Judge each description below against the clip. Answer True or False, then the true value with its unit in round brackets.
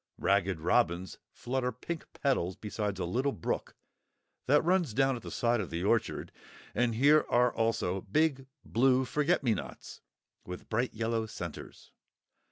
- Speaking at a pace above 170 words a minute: False (150 wpm)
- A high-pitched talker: False (115 Hz)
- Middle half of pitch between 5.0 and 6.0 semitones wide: True (5.3 semitones)